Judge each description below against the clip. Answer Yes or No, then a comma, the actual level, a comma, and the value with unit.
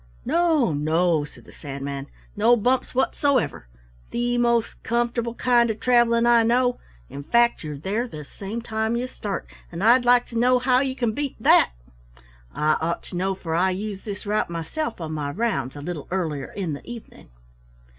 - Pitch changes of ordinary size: No, wide, 6.6 semitones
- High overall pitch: Yes, high, 220 Hz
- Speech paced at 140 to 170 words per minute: No, average, 180 wpm